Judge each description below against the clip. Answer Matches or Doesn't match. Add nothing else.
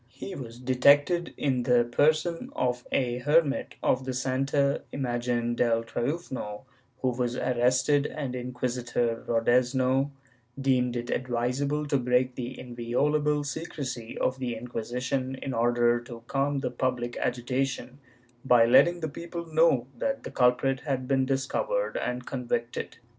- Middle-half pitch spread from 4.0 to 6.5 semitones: Doesn't match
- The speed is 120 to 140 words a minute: Matches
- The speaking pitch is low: Matches